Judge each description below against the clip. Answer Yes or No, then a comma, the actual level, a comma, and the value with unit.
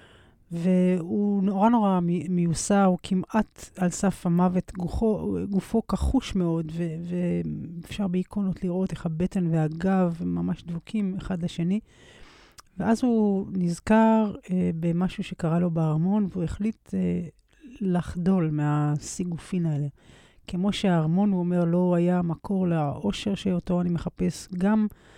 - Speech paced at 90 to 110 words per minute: No, average, 120 wpm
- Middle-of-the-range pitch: Yes, medium, 180 Hz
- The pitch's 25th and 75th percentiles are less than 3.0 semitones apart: Yes, narrow, 2.5 semitones